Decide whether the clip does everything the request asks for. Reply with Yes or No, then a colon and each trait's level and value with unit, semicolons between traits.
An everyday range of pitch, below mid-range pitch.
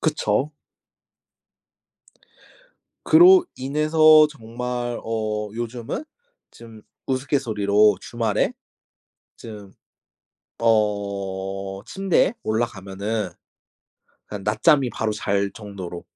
Yes: average, 4.2 semitones; low, 110 Hz